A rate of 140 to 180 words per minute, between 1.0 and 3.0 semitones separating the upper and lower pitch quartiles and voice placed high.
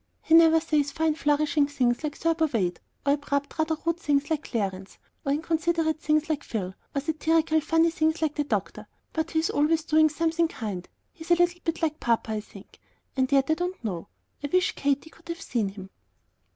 No: average, 195 wpm; average, 2.7 semitones; very high, 310 Hz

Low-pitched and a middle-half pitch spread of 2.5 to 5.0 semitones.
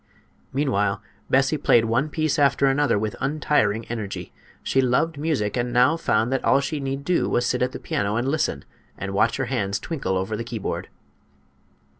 Yes: low, 125 Hz; average, 4.6 semitones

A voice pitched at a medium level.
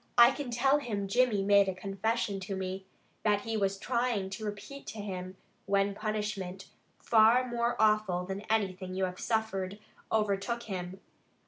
No: high, 205 Hz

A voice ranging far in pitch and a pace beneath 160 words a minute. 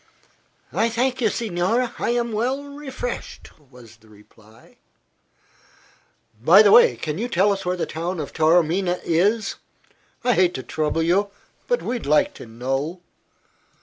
Yes: wide, 7.2 semitones; average, 150 wpm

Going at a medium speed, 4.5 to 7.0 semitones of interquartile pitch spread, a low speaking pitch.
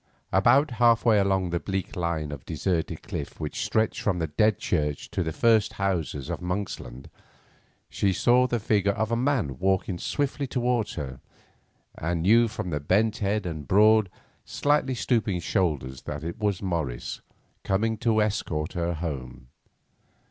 Yes: average, 155 wpm; wide, 5.4 semitones; very low, 95 Hz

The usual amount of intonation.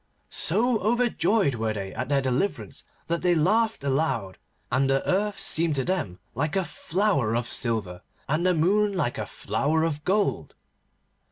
No: wide, 7.1 semitones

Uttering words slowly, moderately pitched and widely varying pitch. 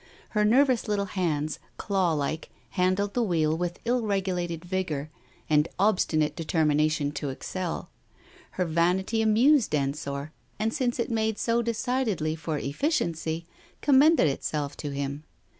Yes: slow, 130 wpm; medium, 175 Hz; wide, 6.1 semitones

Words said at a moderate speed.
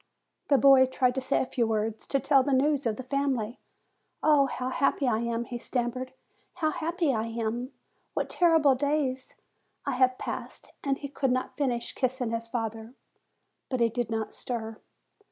Yes: average, 180 wpm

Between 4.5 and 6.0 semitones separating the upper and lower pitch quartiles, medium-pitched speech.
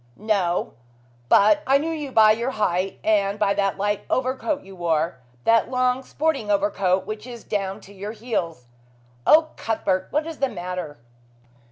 No: average, 4.8 semitones; high, 210 Hz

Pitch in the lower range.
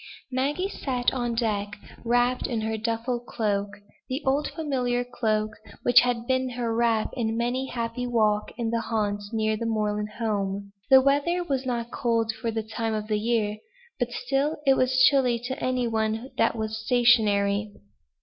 No: high, 235 Hz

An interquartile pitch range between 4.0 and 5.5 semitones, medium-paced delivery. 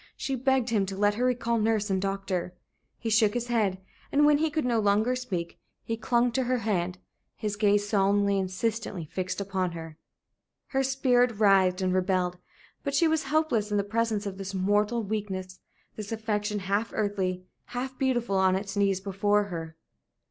No: average, 3.6 semitones; average, 175 wpm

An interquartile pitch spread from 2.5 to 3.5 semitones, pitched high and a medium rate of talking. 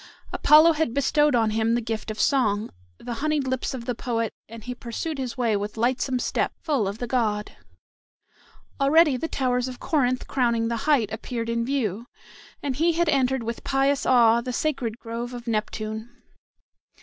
Yes: average, 3.1 semitones; high, 245 Hz; average, 175 wpm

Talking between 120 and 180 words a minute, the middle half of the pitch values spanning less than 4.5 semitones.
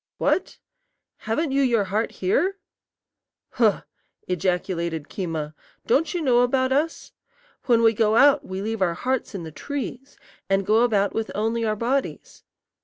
No: average, 150 wpm; average, 5.2 semitones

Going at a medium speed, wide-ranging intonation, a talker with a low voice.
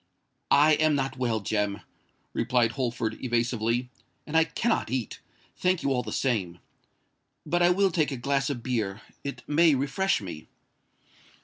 No: average, 145 wpm; average, 4.7 semitones; low, 130 Hz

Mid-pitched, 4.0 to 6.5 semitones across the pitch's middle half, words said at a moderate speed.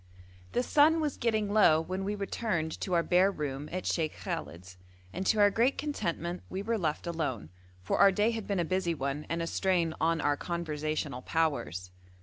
Yes: medium, 170 Hz; average, 4.8 semitones; average, 190 wpm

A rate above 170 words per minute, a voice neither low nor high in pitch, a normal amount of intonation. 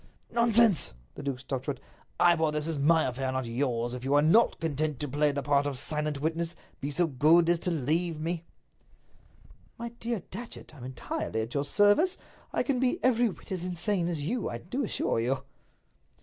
Yes: average, 190 wpm; medium, 155 Hz; average, 4.6 semitones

